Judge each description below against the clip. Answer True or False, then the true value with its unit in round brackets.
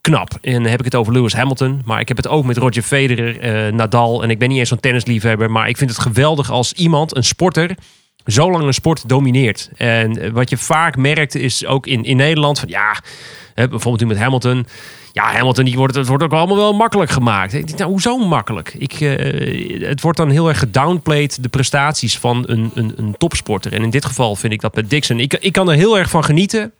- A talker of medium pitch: False (130 Hz)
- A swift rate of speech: True (235 wpm)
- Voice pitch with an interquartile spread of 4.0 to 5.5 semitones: True (4.3 semitones)